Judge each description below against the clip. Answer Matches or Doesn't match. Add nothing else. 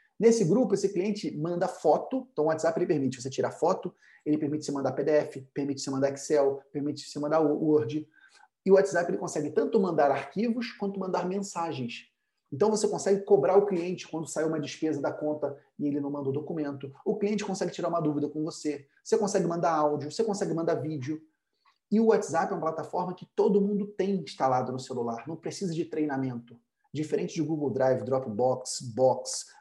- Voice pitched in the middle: Matches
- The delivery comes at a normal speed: Doesn't match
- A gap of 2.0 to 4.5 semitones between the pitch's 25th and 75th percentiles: Doesn't match